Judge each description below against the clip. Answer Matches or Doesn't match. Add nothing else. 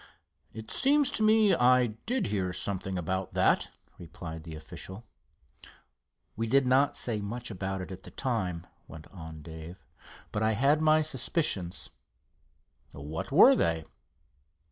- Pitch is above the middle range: Doesn't match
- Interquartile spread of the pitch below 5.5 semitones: Doesn't match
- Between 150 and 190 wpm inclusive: Doesn't match